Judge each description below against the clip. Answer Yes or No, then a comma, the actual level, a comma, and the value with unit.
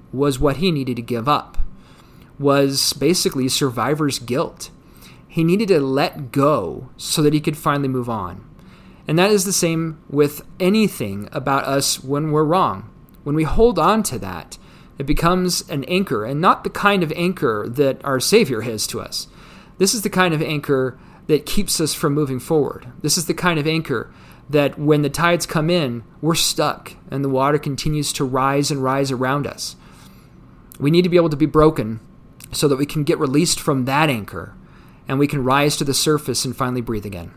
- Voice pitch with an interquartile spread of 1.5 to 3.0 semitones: No, average, 3.5 semitones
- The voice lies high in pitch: No, medium, 150 Hz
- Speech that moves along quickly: No, average, 195 wpm